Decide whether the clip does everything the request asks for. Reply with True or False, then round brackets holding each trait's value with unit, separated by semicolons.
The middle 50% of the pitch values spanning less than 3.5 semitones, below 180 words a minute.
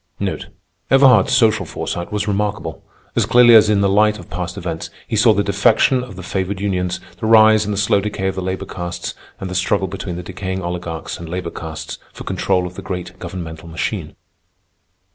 False (2.9 semitones; 195 wpm)